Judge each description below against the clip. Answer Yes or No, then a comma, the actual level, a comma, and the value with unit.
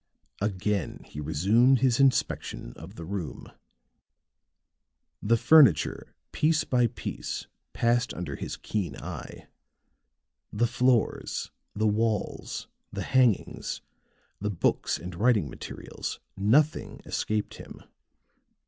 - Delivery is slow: Yes, slow, 105 wpm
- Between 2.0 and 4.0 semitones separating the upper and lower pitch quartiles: No, average, 4.7 semitones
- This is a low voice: Yes, low, 110 Hz